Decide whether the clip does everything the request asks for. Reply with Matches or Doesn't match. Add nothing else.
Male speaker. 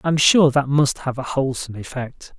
Matches